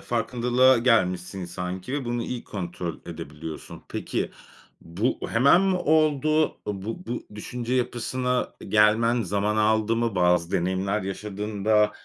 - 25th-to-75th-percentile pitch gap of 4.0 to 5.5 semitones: Yes, average, 4.6 semitones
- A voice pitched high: No, low, 110 Hz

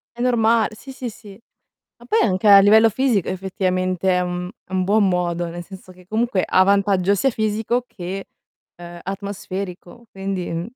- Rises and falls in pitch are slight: No, average, 3.1 semitones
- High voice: Yes, high, 195 Hz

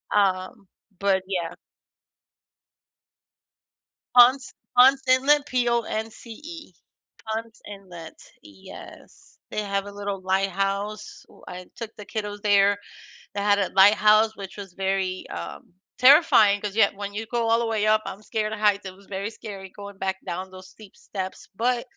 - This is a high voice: Yes, high, 205 Hz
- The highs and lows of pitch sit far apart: No, narrow, 2.5 semitones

